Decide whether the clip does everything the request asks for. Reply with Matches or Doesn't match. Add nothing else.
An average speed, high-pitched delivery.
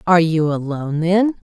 Doesn't match